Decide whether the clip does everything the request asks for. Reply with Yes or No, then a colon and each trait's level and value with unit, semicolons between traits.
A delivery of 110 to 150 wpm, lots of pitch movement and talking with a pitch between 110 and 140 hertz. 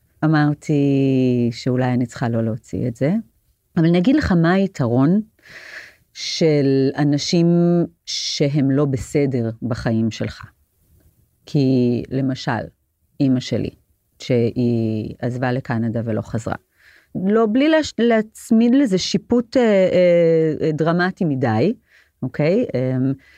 No: slow, 100 wpm; wide, 6.4 semitones; low, 135 Hz